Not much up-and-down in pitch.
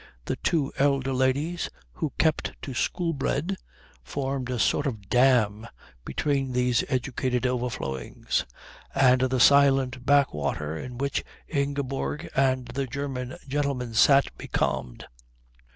Yes: narrow, 2.1 semitones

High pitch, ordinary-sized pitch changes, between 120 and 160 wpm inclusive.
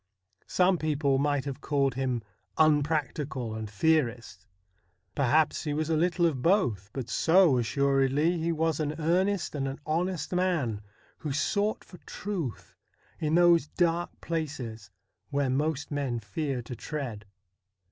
No: medium, 150 Hz; average, 4.0 semitones; average, 150 wpm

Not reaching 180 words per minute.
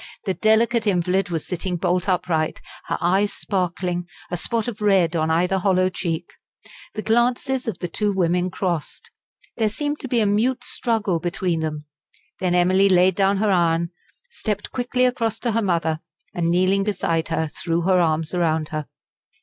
Yes: average, 170 wpm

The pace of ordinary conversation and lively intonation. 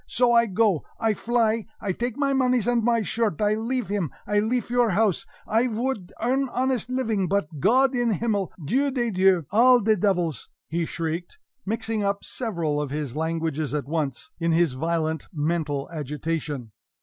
Yes: average, 175 wpm; wide, 6.5 semitones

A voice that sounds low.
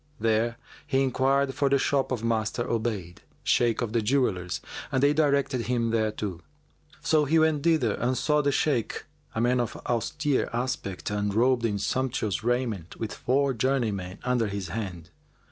Yes: low, 120 Hz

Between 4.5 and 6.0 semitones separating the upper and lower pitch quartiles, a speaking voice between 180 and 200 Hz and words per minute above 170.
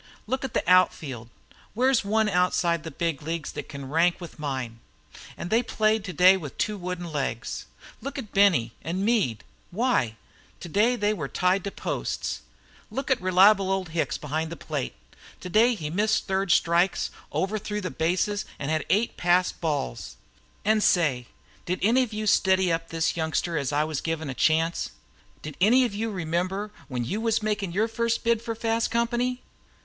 Yes: average, 5.1 semitones; medium, 185 Hz; average, 180 wpm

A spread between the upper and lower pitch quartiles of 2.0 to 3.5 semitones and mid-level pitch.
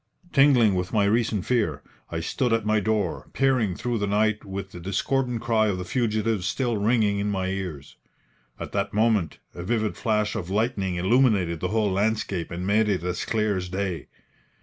No: average, 3.1 semitones; low, 105 Hz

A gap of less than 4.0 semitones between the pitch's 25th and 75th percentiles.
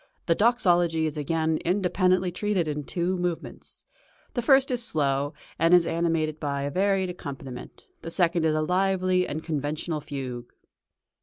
Yes: average, 3.4 semitones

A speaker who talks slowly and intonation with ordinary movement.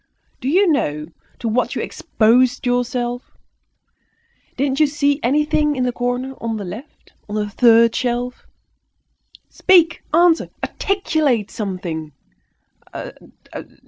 Yes: slow, 110 wpm; average, 4.6 semitones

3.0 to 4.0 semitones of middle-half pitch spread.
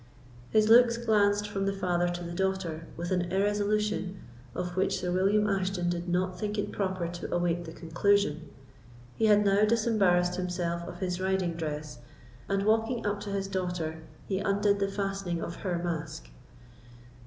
No: narrow, 2.6 semitones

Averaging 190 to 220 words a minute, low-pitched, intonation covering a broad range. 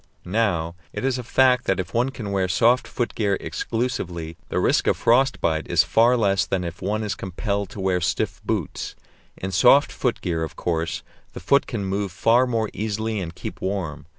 No: average, 200 wpm; low, 100 Hz; average, 4.4 semitones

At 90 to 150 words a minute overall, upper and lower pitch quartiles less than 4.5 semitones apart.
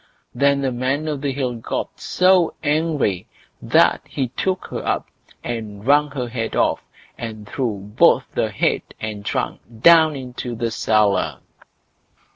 No: average, 140 wpm; average, 4.8 semitones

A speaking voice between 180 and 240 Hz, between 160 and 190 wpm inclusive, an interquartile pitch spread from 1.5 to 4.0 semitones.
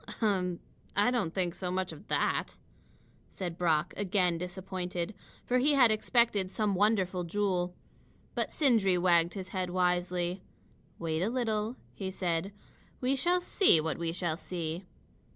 No: medium, 185 Hz; average, 145 wpm; average, 3.2 semitones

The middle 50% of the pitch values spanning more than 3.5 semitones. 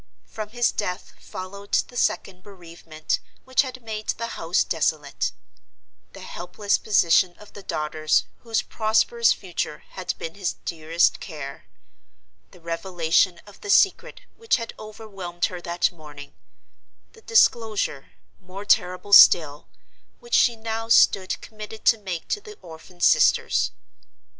Yes: average, 4.7 semitones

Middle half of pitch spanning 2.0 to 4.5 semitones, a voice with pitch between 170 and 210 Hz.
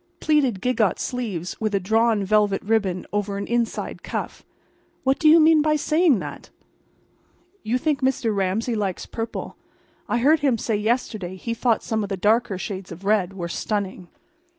No: average, 4.1 semitones; high, 220 Hz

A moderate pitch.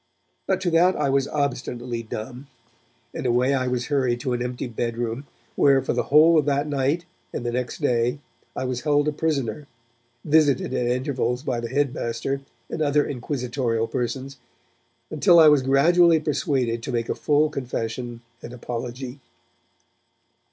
No: low, 130 Hz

